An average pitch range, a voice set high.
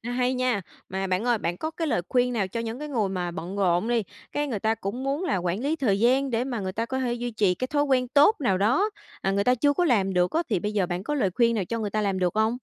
Yes: average, 4.8 semitones; high, 230 Hz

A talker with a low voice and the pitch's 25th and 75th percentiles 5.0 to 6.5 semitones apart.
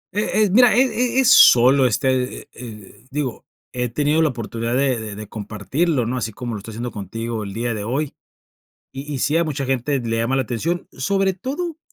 Yes: low, 130 Hz; wide, 5.4 semitones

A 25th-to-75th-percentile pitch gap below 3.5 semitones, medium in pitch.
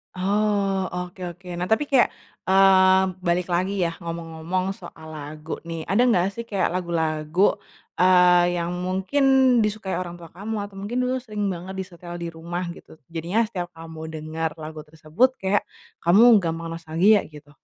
Yes: average, 2.8 semitones; medium, 180 Hz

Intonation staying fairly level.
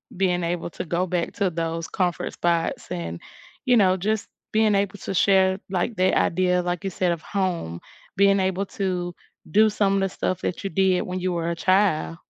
Yes: narrow, 2.1 semitones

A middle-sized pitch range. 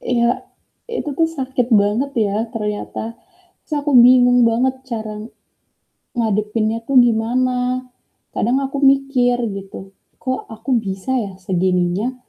Yes: average, 3.3 semitones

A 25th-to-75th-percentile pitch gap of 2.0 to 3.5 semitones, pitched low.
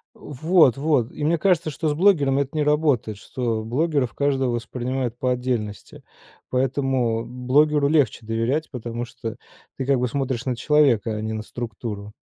No: average, 4.0 semitones; low, 130 Hz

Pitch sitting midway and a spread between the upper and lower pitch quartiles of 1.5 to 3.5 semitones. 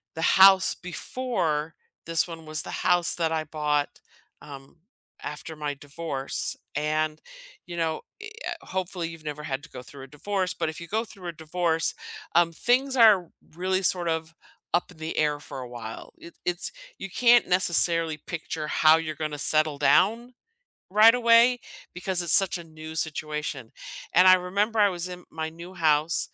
Yes: medium, 165 Hz; average, 3.2 semitones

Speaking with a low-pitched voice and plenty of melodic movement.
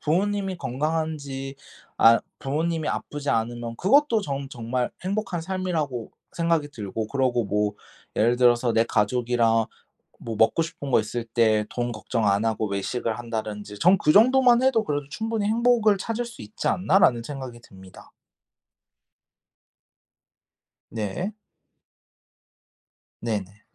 Yes: low, 130 Hz; wide, 7.9 semitones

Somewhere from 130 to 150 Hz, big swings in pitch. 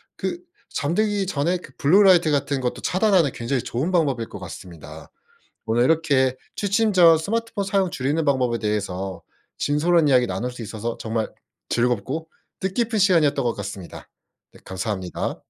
Yes: medium, 140 Hz; wide, 7.8 semitones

